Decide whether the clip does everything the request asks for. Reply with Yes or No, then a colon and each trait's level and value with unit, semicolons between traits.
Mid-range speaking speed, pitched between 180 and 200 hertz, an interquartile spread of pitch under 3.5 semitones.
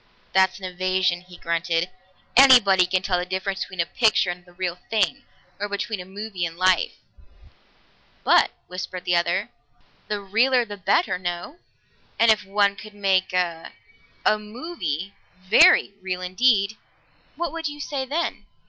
Yes: average, 155 wpm; high, 190 Hz; average, 3.0 semitones